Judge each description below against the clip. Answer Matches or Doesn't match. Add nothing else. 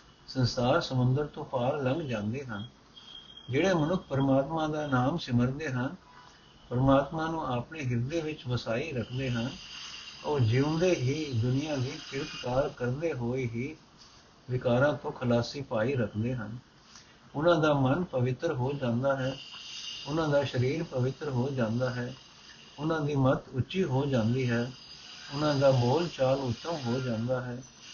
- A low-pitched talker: Matches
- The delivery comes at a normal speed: Matches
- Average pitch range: Matches